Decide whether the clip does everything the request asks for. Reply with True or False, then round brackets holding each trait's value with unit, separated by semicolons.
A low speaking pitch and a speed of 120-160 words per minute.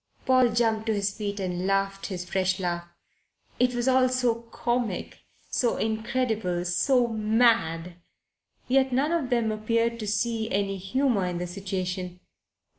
False (220 Hz; 145 wpm)